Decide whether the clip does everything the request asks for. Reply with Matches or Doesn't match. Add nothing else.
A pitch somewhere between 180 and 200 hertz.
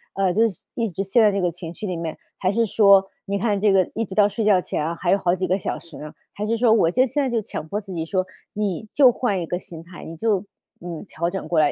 Matches